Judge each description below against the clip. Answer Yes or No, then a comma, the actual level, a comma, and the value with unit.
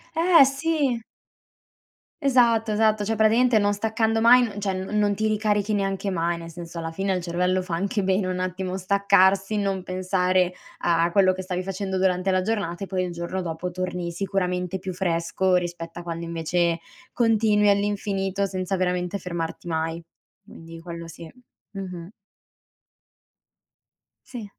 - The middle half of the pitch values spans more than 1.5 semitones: Yes, average, 2.8 semitones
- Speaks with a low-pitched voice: No, high, 190 Hz